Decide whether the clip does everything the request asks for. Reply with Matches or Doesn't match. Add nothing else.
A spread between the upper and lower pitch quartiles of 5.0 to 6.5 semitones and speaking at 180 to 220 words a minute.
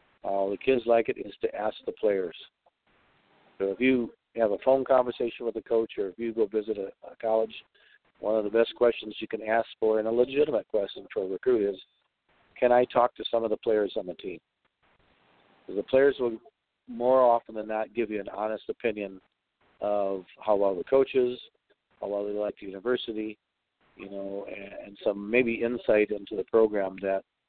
Doesn't match